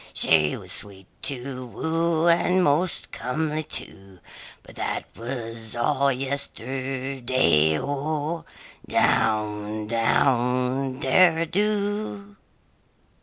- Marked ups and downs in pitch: Yes, wide, 5.8 semitones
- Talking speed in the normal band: No, slow, 85 wpm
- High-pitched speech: No, low, 135 Hz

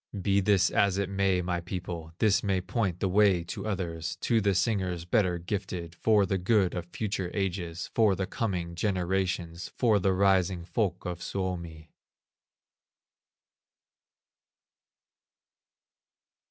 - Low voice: Yes, very low, 95 Hz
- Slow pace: Yes, slow, 125 wpm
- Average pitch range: No, narrow, 2.2 semitones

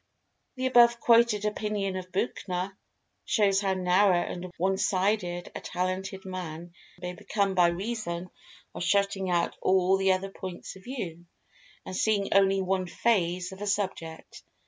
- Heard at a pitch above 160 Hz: Yes, high, 190 Hz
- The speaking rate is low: No, average, 145 wpm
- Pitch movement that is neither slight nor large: No, narrow, 2.1 semitones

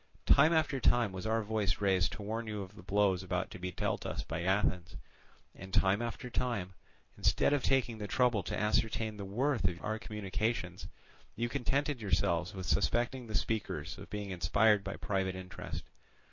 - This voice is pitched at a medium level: No, low, 105 Hz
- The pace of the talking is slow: No, average, 180 wpm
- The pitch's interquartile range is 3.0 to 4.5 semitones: Yes, average, 3.7 semitones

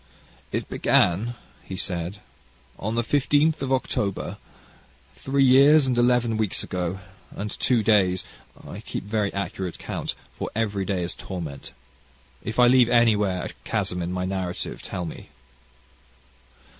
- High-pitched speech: No, low, 105 Hz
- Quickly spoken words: No, average, 140 wpm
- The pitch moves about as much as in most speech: Yes, average, 4.9 semitones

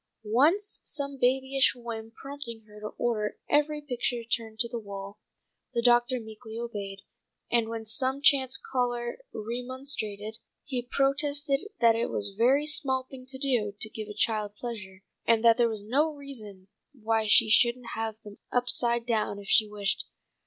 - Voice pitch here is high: Yes, high, 235 Hz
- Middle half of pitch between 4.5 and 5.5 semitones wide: No, average, 3.4 semitones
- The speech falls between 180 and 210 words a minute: No, average, 165 wpm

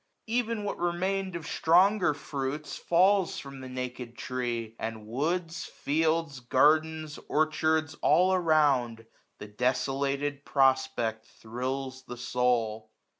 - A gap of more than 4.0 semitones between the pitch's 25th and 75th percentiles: Yes, average, 4.7 semitones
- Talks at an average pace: No, slow, 115 wpm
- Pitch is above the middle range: No, medium, 140 Hz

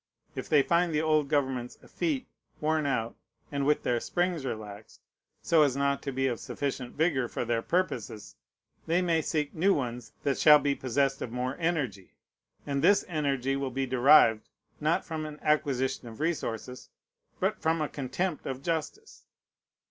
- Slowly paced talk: No, average, 165 wpm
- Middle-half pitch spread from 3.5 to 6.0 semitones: Yes, average, 3.8 semitones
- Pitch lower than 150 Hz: Yes, medium, 140 Hz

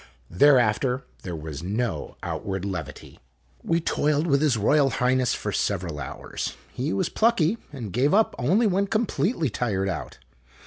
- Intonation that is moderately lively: No, wide, 8.3 semitones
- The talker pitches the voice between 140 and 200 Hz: No, low, 130 Hz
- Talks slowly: No, average, 145 wpm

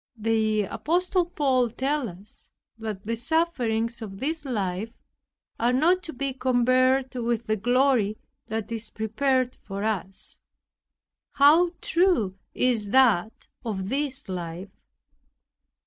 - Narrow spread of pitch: No, average, 4.1 semitones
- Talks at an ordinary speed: No, slow, 115 wpm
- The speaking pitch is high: Yes, high, 240 Hz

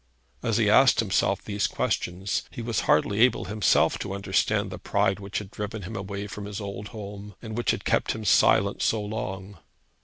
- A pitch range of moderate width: No, narrow, 1.6 semitones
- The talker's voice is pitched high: No, low, 100 Hz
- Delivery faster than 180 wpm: Yes, average, 190 wpm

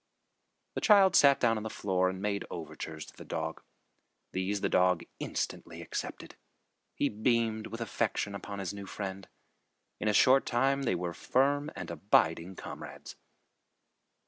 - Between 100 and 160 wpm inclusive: Yes, average, 150 wpm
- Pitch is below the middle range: Yes, low, 100 Hz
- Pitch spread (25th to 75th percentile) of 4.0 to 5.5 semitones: Yes, average, 4.6 semitones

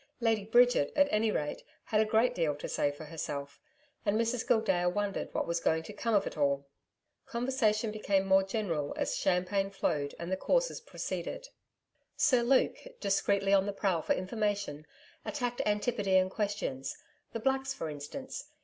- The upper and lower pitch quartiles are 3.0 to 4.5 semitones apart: No, average, 5.1 semitones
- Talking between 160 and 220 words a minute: Yes, average, 165 wpm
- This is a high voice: Yes, high, 200 Hz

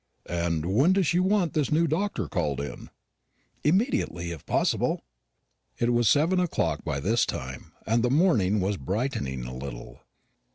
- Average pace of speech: Yes, average, 155 wpm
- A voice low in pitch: Yes, low, 110 Hz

